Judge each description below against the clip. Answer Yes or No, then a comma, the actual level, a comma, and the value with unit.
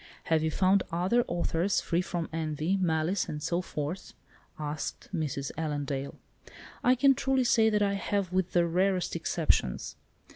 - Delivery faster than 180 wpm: No, average, 150 wpm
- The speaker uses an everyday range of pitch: Yes, average, 4.0 semitones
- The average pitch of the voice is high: No, medium, 175 Hz